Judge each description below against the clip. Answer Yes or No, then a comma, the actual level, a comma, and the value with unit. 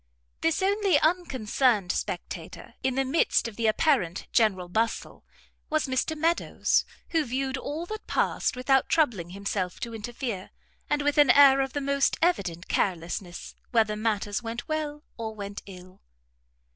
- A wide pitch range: Yes, wide, 6.2 semitones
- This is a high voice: Yes, very high, 250 Hz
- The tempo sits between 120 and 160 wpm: Yes, average, 145 wpm